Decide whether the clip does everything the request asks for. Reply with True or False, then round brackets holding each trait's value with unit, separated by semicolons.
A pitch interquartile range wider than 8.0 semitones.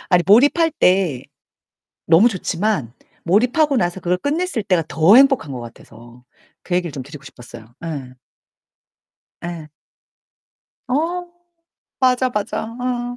True (9.0 semitones)